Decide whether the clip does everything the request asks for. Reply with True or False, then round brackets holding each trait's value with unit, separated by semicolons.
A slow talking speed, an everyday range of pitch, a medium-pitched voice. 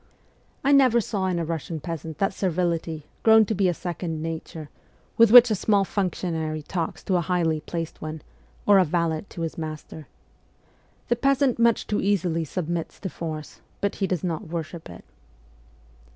False (170 wpm; 3.9 semitones; 175 Hz)